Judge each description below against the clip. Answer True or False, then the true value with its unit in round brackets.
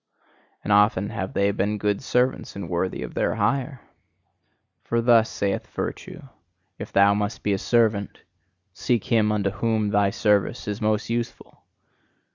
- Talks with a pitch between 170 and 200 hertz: False (105 Hz)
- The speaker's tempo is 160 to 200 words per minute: False (150 wpm)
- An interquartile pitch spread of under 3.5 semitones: True (2.4 semitones)